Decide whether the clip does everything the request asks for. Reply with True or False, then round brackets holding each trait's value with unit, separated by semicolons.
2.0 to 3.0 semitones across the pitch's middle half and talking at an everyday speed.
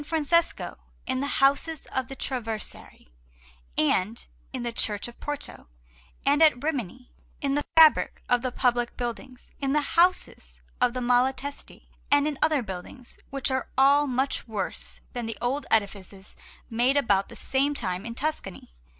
False (3.5 semitones; 155 wpm)